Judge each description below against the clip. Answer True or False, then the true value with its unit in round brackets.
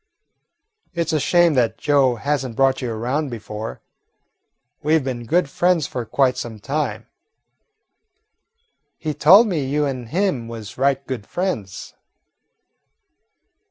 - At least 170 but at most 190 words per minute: False (135 wpm)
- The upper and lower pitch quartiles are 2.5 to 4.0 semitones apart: False (4.6 semitones)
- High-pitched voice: False (135 Hz)